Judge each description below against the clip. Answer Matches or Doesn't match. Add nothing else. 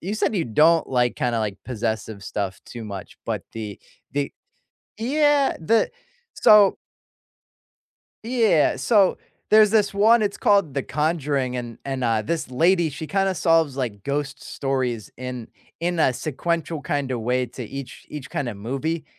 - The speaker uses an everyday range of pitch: Doesn't match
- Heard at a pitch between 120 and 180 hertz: Matches